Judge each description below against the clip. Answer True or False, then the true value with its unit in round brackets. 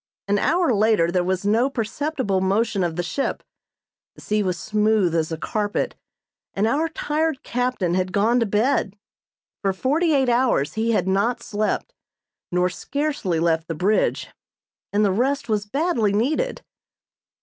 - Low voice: False (215 Hz)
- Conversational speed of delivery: True (155 wpm)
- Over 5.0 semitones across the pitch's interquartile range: True (5.5 semitones)